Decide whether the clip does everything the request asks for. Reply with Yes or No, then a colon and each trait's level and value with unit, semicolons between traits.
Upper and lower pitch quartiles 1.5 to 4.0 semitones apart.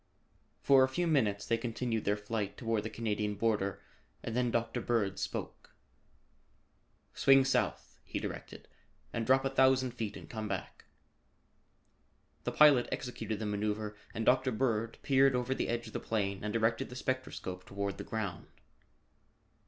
Yes: average, 3.5 semitones